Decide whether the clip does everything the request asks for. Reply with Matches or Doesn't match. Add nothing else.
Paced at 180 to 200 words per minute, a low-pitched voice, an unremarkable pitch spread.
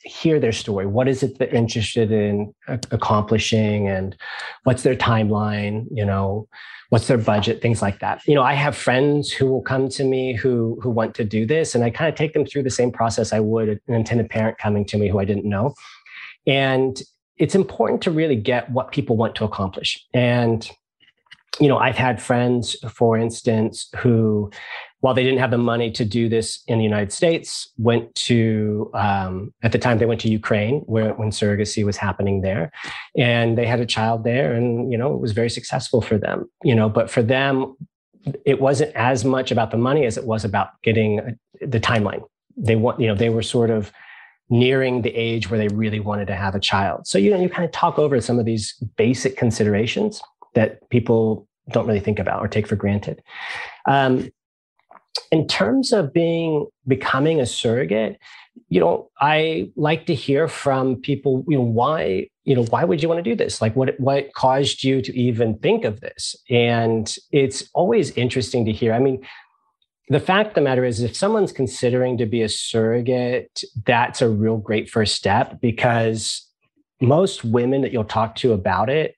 Matches